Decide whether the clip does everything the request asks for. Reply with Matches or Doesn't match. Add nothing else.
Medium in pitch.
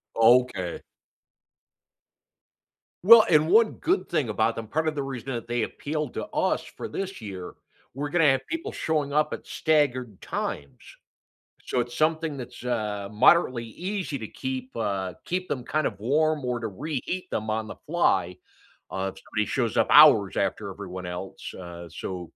Doesn't match